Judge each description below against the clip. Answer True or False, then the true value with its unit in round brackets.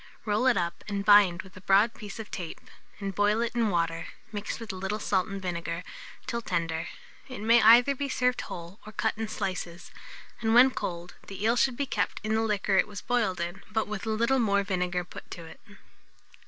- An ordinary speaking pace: False (215 wpm)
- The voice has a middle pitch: False (205 Hz)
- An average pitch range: True (3.6 semitones)